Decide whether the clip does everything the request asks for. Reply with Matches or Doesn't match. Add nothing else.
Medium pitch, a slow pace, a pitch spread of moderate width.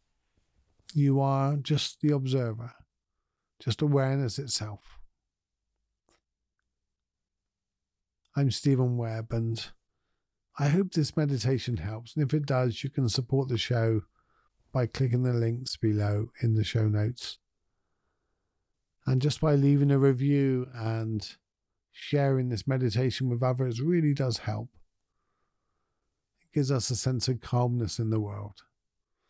Doesn't match